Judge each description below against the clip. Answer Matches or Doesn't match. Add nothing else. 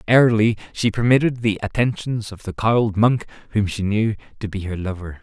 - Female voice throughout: Doesn't match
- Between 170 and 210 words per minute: Matches